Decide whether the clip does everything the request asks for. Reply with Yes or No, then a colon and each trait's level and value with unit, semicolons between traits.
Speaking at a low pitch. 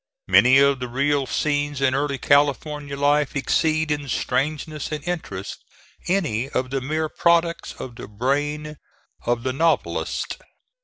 No: medium, 145 Hz